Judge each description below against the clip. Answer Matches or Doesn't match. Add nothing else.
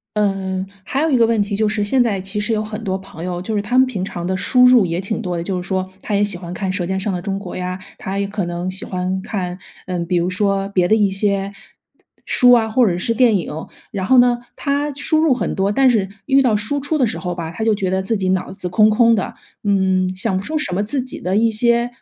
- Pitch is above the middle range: Matches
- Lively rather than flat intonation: Doesn't match